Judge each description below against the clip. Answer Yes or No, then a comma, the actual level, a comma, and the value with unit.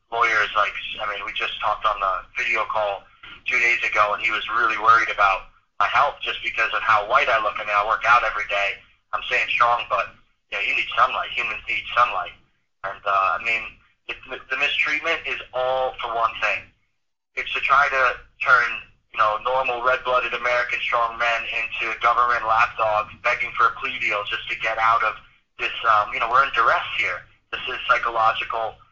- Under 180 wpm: No, average, 195 wpm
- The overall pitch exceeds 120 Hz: No, low, 115 Hz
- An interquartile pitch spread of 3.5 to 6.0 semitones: No, average, 3.1 semitones